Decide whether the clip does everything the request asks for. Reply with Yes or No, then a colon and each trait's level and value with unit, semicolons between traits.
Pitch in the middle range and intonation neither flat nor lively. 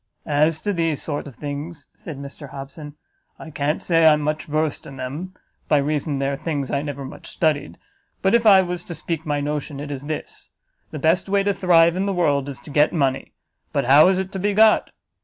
Yes: medium, 150 Hz; average, 3.3 semitones